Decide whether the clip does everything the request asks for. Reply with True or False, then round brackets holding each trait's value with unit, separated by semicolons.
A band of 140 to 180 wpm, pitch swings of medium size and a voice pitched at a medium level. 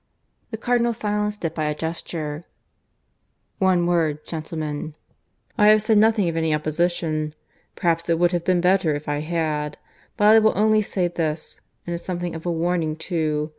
True (175 wpm; 3.4 semitones; 170 Hz)